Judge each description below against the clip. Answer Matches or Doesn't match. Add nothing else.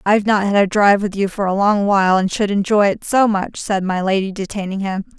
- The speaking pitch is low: Doesn't match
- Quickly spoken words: Matches